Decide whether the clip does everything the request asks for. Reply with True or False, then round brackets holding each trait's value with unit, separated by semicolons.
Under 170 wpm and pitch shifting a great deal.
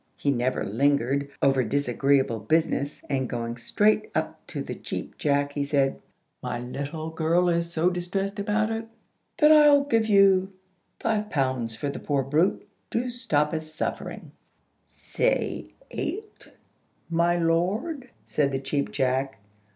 True (140 wpm; 6.5 semitones)